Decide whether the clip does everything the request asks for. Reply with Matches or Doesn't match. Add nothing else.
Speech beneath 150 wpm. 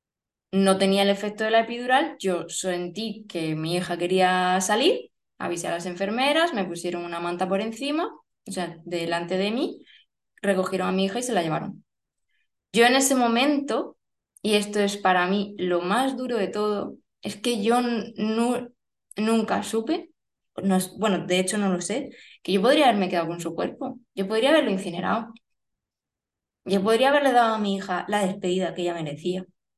Doesn't match